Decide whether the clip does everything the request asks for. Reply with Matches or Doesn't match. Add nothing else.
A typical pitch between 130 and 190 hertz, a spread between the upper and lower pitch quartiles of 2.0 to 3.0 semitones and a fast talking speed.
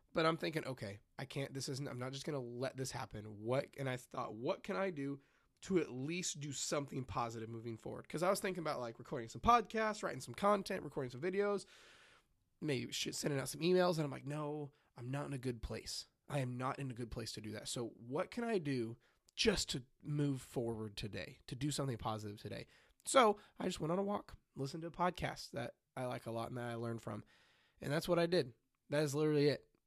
Doesn't match